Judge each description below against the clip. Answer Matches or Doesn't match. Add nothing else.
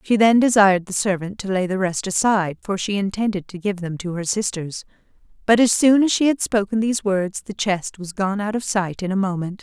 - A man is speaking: Doesn't match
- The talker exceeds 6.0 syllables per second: Doesn't match